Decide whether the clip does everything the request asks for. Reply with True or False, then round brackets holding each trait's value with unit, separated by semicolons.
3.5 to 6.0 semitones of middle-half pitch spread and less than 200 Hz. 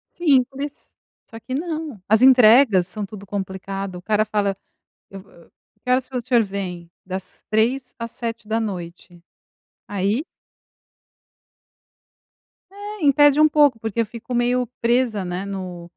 False (4.7 semitones; 220 Hz)